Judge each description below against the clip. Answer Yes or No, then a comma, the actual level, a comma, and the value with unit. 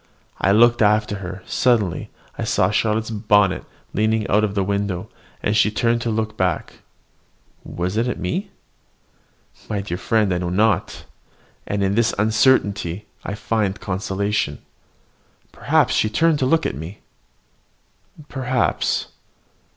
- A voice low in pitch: Yes, low, 105 Hz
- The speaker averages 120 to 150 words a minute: Yes, slow, 135 wpm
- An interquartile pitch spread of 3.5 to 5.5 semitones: No, narrow, 2.4 semitones